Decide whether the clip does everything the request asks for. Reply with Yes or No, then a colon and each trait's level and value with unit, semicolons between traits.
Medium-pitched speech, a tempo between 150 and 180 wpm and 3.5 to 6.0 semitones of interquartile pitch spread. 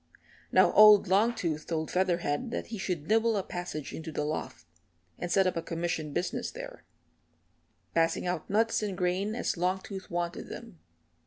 Yes: medium, 180 Hz; average, 160 wpm; average, 3.9 semitones